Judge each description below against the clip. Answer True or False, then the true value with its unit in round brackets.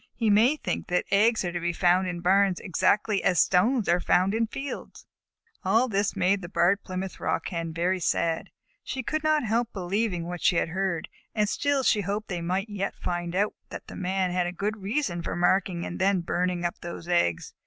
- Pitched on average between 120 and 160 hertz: False (190 Hz)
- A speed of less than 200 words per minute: False (205 wpm)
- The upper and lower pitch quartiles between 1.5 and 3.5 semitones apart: True (3.2 semitones)